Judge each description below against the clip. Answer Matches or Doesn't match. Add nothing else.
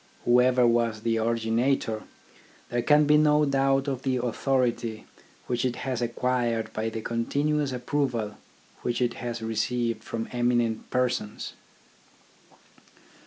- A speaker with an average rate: Doesn't match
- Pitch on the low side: Matches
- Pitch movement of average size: Doesn't match